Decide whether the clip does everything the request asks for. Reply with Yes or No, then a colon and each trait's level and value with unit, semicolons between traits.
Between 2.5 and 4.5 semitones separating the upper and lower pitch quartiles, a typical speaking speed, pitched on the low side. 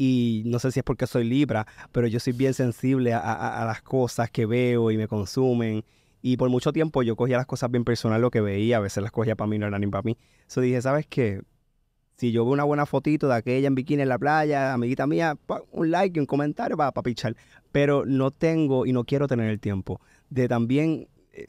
No: average, 3.1 semitones; fast, 235 wpm; low, 125 Hz